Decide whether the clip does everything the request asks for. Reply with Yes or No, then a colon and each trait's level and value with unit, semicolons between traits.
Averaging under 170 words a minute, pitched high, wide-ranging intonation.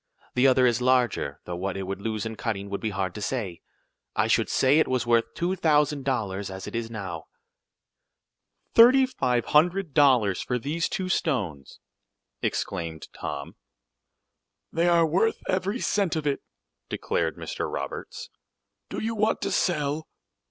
No: average, 160 wpm; low, 125 Hz; wide, 8.5 semitones